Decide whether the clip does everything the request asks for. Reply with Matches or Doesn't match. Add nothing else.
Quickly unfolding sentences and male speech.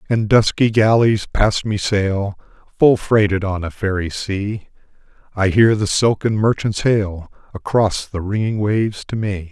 Doesn't match